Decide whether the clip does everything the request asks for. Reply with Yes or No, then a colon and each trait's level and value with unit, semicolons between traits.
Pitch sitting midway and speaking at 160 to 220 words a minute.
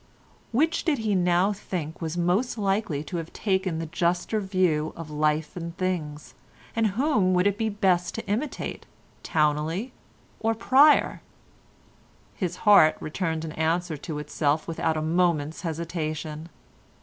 No: medium, 175 Hz; slow, 135 wpm